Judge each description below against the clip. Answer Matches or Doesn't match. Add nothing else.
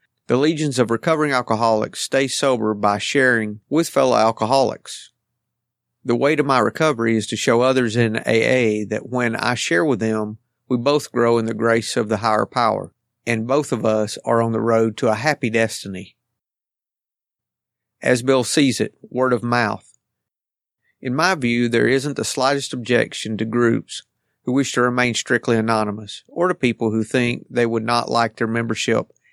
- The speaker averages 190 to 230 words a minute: Doesn't match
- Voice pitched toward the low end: Matches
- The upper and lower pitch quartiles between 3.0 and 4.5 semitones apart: Doesn't match